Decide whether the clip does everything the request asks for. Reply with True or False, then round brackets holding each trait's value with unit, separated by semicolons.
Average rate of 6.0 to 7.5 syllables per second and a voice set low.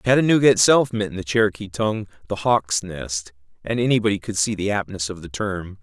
False (5.8 syllables/s; 100 Hz)